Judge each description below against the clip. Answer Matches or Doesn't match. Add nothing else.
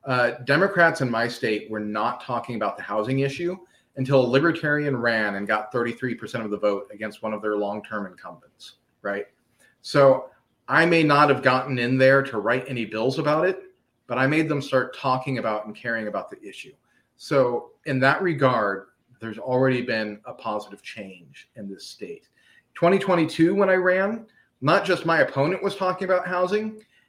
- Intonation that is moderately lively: Doesn't match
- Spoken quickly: Doesn't match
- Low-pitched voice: Matches